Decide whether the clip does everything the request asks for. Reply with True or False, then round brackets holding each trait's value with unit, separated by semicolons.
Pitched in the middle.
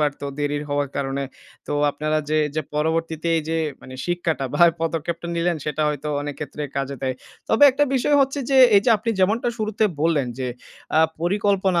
True (160 Hz)